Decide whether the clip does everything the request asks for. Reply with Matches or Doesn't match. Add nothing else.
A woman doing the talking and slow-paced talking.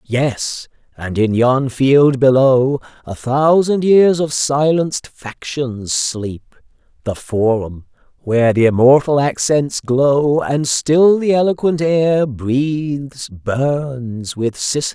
Doesn't match